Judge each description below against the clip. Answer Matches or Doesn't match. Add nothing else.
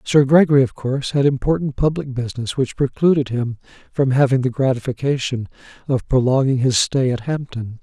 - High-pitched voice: Doesn't match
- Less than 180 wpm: Matches